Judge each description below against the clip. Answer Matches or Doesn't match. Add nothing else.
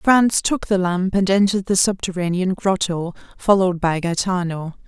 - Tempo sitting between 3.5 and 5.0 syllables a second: Matches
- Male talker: Doesn't match